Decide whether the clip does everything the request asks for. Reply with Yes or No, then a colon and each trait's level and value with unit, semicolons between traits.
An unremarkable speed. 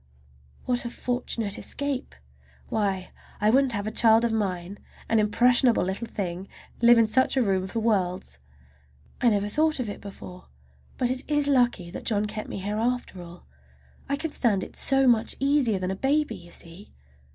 Yes: average, 180 wpm